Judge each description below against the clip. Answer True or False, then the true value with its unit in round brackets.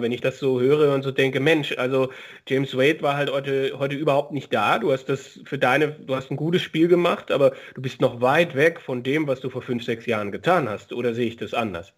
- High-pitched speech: False (135 Hz)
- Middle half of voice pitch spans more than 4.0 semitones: False (2.7 semitones)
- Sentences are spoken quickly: True (255 wpm)